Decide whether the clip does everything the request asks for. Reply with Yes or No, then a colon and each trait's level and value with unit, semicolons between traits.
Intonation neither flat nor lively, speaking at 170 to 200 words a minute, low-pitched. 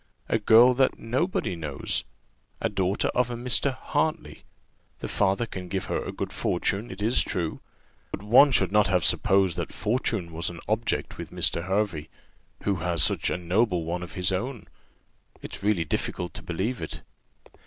Yes: average, 5.0 semitones; average, 175 wpm; low, 100 Hz